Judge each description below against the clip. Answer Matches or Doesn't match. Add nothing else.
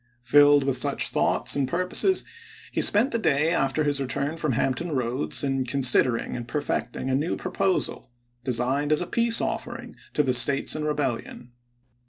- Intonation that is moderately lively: Matches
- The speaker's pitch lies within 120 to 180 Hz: Matches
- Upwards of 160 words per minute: Matches